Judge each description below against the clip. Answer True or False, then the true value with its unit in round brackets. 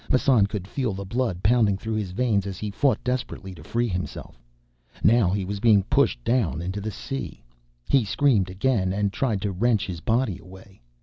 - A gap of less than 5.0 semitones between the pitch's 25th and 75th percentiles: True (4.2 semitones)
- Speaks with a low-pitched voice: True (105 Hz)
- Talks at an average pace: True (190 wpm)